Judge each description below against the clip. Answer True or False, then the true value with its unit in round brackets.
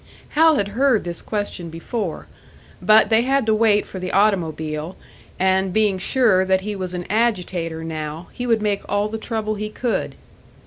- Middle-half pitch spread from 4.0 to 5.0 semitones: False (3.5 semitones)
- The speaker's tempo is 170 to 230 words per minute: True (175 wpm)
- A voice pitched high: True (205 Hz)